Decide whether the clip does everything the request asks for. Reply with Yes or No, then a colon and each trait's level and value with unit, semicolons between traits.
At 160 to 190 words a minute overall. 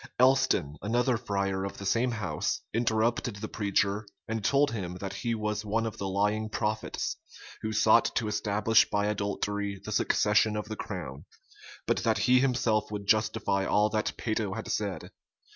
Yes: average, 165 wpm